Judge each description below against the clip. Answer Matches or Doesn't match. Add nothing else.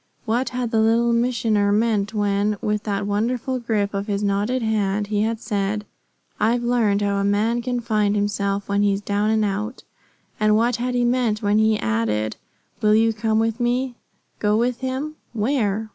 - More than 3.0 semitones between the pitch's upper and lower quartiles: Doesn't match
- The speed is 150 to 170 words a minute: Doesn't match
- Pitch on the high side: Matches